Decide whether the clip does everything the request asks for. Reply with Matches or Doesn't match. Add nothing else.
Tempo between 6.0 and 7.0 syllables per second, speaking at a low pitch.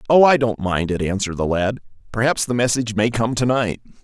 Matches